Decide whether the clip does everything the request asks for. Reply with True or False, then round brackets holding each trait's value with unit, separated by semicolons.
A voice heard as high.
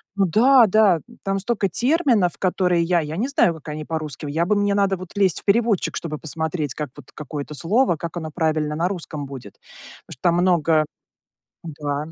False (170 Hz)